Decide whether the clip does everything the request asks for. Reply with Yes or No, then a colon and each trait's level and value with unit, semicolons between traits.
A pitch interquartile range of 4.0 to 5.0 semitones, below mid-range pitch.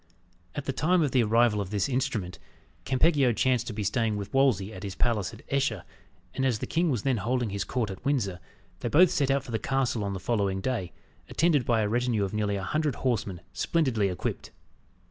Yes: average, 4.7 semitones; low, 120 Hz